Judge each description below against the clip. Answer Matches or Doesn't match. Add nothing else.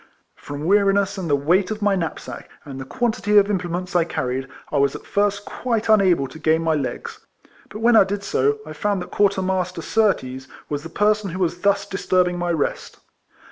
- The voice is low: Doesn't match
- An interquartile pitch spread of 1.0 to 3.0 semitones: Doesn't match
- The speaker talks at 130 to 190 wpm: Doesn't match